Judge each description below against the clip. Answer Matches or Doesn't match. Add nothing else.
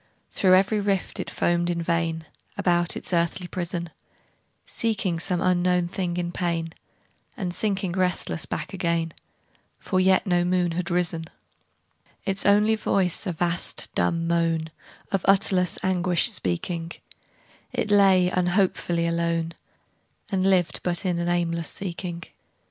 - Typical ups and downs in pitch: Doesn't match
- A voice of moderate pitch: Matches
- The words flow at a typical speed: Doesn't match